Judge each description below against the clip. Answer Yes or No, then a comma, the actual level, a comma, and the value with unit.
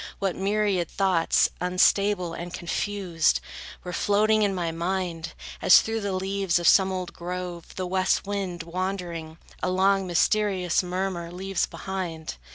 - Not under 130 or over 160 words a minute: Yes, average, 140 wpm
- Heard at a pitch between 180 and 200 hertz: Yes, medium, 185 Hz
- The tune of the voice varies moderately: No, narrow, 2.1 semitones